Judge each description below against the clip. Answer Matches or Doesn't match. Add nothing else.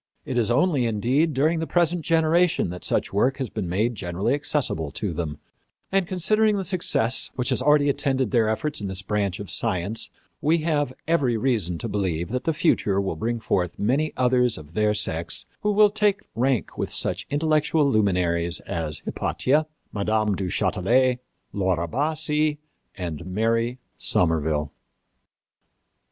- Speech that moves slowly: Doesn't match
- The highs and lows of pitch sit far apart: Matches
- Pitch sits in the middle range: Doesn't match